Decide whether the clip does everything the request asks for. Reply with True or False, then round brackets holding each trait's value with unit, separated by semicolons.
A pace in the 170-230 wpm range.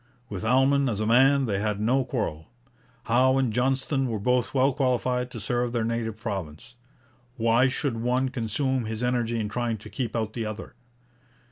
True (175 wpm)